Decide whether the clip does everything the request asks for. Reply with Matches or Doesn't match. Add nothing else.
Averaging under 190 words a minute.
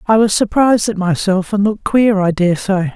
Doesn't match